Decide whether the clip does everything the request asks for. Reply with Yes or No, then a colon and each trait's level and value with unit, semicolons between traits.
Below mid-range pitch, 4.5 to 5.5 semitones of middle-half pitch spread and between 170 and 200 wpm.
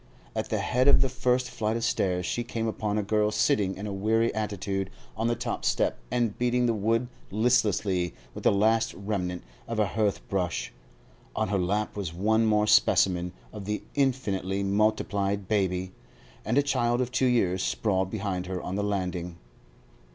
No: low, 105 Hz; average, 3.1 semitones; average, 180 wpm